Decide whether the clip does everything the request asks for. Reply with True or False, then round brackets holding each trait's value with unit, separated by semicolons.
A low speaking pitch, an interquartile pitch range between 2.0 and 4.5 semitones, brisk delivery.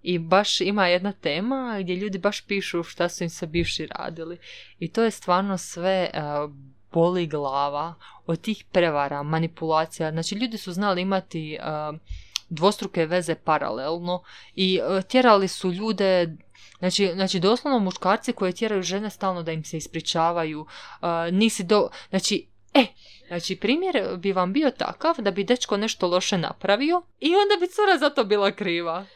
False (185 Hz; 3.6 semitones; 165 wpm)